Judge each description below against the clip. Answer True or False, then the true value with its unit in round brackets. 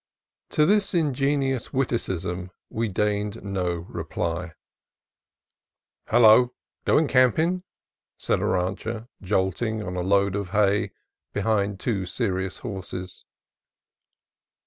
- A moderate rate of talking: False (100 wpm)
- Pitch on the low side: True (105 Hz)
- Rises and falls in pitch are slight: False (4.7 semitones)